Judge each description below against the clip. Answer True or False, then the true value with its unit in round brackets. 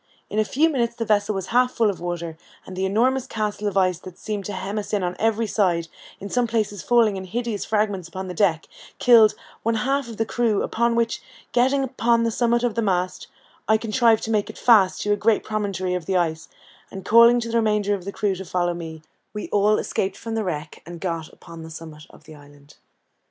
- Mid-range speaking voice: False (205 Hz)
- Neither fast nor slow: False (230 wpm)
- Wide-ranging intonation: False (4.0 semitones)